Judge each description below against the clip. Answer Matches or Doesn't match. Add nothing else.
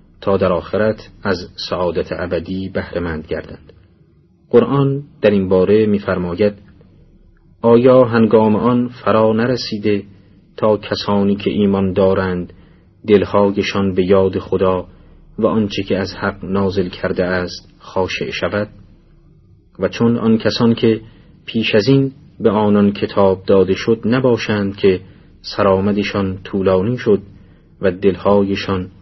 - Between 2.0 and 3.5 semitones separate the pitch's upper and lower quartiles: Matches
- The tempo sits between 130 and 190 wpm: Doesn't match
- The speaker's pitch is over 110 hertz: Doesn't match